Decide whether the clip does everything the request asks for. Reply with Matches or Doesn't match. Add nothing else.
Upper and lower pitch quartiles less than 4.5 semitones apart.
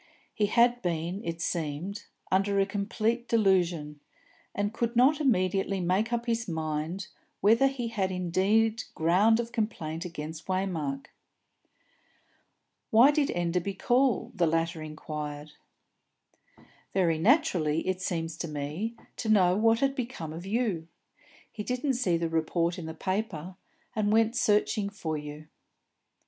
Doesn't match